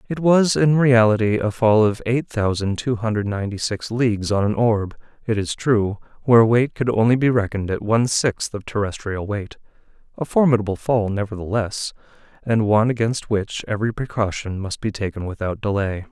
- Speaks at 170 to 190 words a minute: Yes, average, 175 wpm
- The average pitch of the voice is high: No, low, 110 Hz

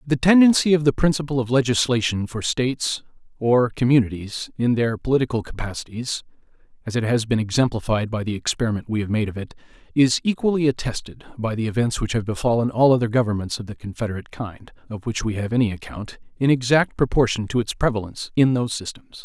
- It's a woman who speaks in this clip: No, male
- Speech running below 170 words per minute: No, average, 185 wpm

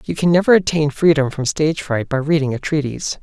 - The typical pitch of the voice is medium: Yes, medium, 150 Hz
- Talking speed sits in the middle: No, fast, 225 wpm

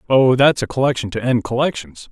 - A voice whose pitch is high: No, low, 125 Hz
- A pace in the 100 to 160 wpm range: No, average, 200 wpm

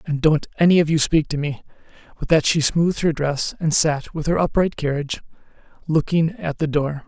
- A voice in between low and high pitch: Yes, medium, 155 Hz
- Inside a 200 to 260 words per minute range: Yes, fast, 205 wpm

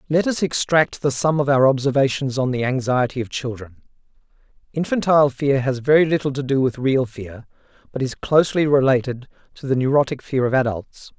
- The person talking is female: No, male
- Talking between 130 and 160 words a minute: No, average, 175 wpm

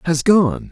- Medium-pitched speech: Yes, medium, 155 Hz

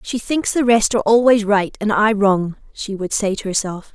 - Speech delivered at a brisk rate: Yes, fast, 230 wpm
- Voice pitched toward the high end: Yes, high, 210 Hz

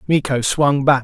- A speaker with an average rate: Yes, average, 175 wpm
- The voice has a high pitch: No, medium, 140 Hz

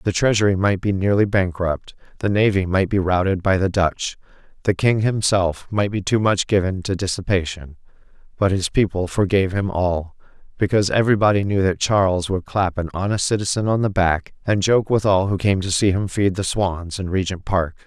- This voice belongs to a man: Yes, male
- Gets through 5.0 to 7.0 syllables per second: Yes, 5.3 syllables/s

